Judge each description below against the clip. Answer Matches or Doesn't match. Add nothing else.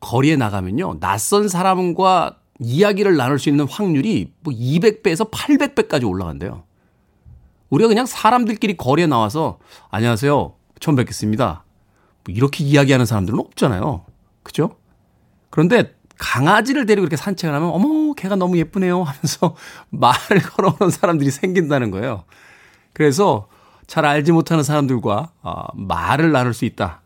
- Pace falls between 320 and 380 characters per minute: Matches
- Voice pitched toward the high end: Doesn't match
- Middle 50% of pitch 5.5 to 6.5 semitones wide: Doesn't match